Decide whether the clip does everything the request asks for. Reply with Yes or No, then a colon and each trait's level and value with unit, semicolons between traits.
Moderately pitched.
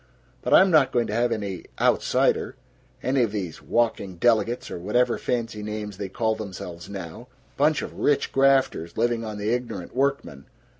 No: low, 110 Hz